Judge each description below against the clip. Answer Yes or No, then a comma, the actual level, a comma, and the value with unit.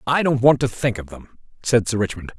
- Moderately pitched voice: No, low, 115 Hz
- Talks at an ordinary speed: No, fast, 250 wpm